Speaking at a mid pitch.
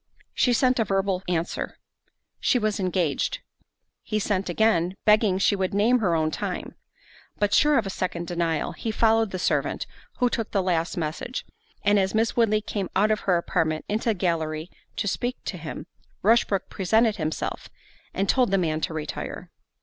No: high, 195 Hz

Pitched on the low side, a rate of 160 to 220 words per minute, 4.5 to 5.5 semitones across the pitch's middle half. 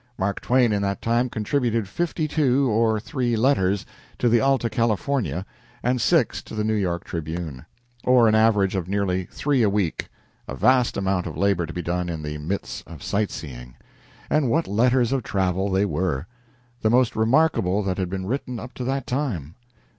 Yes: low, 105 Hz; average, 185 wpm; average, 5.1 semitones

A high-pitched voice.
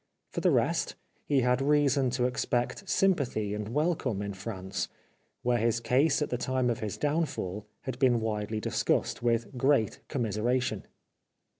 No: low, 125 Hz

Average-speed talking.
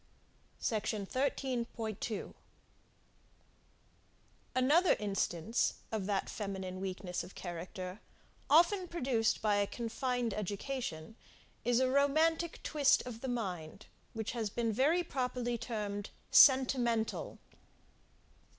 No: slow, 95 wpm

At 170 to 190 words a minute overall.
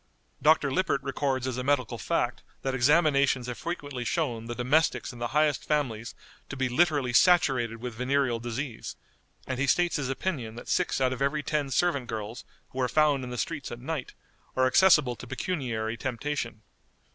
Yes: average, 180 wpm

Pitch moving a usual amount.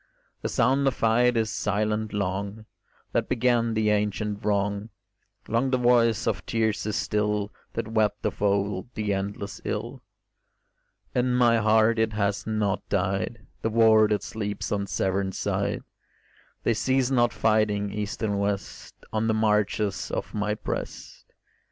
No: narrow, 1.8 semitones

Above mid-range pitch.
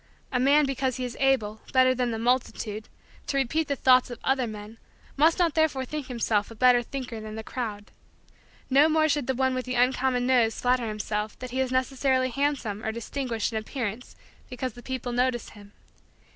Yes: very high, 255 Hz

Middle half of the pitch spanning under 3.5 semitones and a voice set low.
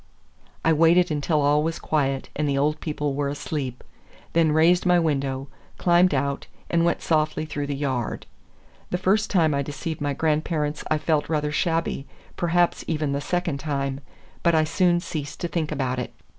No: average, 2.8 semitones; medium, 155 Hz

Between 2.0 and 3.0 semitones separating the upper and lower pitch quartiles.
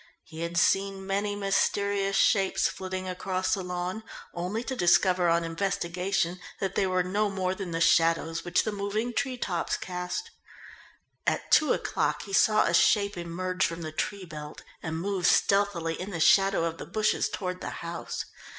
Yes: narrow, 2.6 semitones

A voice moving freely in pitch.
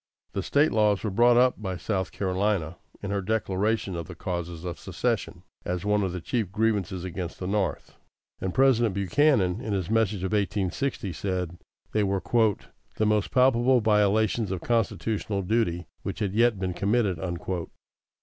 No: average, 3.3 semitones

